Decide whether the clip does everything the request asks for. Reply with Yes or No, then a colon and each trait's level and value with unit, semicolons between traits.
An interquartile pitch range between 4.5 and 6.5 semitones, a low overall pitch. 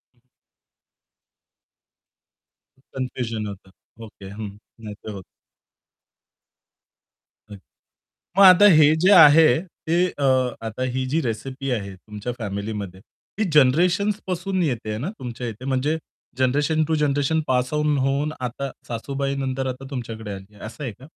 Yes: average, 5.2 semitones; low, 130 Hz